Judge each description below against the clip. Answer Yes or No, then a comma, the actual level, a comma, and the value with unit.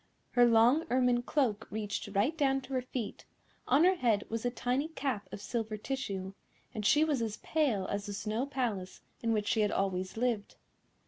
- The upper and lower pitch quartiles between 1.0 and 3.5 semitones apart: No, average, 4.3 semitones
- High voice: Yes, high, 230 Hz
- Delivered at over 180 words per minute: Yes, average, 190 wpm